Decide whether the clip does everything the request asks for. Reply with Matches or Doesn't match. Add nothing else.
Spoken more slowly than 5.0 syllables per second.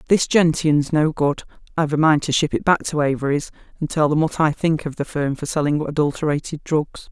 Doesn't match